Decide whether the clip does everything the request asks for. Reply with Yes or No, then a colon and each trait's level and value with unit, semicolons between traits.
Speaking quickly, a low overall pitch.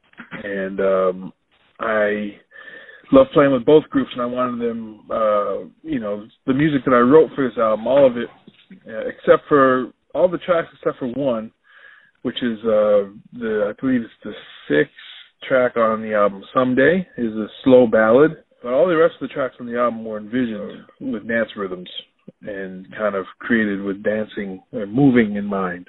No: average, 180 wpm; low, 120 Hz